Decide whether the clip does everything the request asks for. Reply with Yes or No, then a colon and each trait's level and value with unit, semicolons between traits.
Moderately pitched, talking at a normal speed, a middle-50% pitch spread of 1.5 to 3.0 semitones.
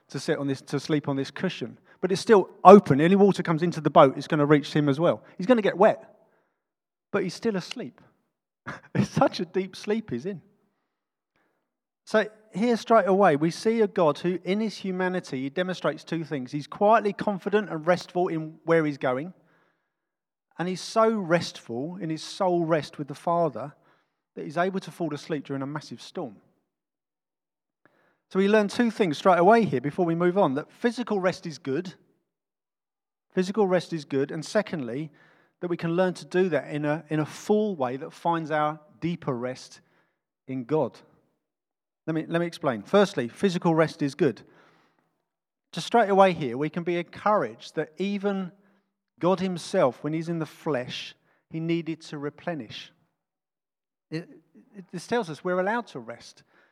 No: medium, 170 Hz; average, 180 wpm; average, 4.4 semitones